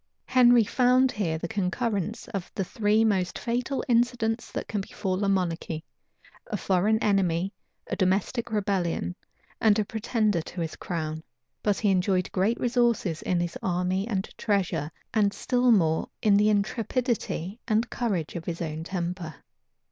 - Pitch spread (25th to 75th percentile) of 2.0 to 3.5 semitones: No, average, 4.0 semitones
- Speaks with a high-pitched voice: Yes, high, 200 Hz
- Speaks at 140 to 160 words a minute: Yes, average, 150 wpm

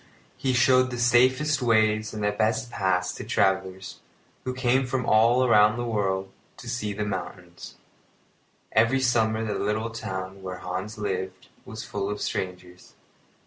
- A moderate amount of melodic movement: Yes, average, 4.2 semitones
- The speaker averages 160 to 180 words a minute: No, average, 145 wpm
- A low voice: Yes, low, 110 Hz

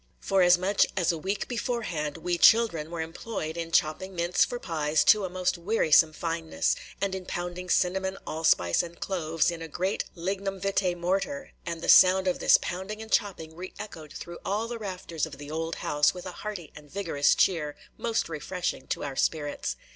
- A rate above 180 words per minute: Yes, average, 190 wpm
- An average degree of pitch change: Yes, average, 3.2 semitones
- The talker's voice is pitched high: No, medium, 175 Hz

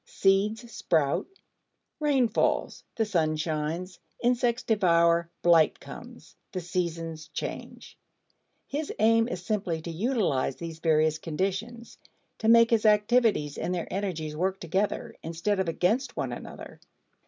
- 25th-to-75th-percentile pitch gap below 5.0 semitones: No, wide, 5.4 semitones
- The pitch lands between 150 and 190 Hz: Yes, medium, 185 Hz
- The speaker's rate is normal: No, slow, 130 wpm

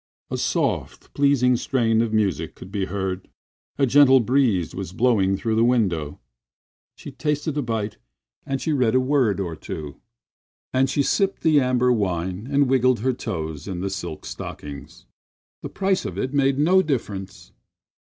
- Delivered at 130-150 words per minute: No, average, 165 wpm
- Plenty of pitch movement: Yes, wide, 6.1 semitones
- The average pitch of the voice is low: Yes, low, 115 Hz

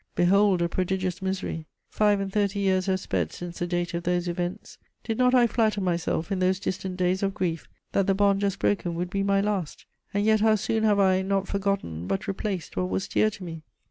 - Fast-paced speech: Yes, fast, 220 wpm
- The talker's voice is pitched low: No, high, 190 Hz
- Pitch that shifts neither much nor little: No, narrow, 2.3 semitones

